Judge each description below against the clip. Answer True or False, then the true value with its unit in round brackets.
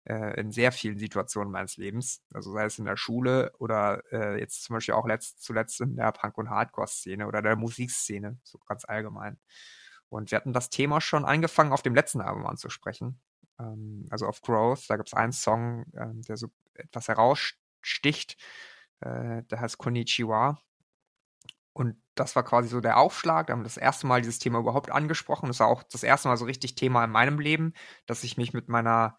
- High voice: False (120 Hz)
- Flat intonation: False (3.2 semitones)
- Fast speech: True (195 wpm)